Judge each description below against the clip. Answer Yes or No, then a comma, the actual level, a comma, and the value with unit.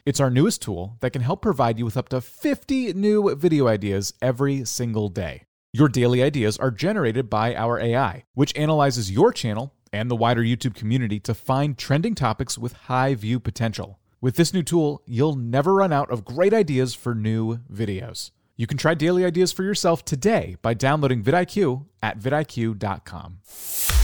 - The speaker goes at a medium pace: Yes, average, 175 wpm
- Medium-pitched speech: No, low, 125 Hz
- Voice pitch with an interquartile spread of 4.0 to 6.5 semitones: Yes, average, 4.6 semitones